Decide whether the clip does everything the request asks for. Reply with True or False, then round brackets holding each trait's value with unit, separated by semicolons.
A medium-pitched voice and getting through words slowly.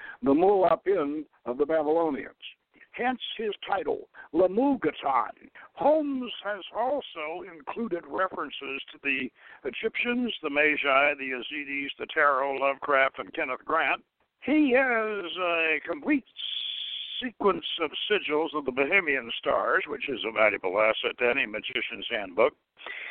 True (165 Hz; 120 wpm)